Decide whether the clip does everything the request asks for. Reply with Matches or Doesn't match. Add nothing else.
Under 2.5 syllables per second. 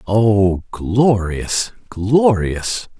Matches